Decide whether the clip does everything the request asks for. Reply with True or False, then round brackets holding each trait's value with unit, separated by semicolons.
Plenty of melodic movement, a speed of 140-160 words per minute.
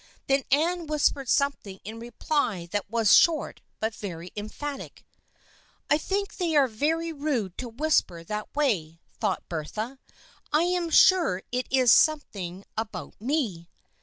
True (7.1 semitones; 150 wpm)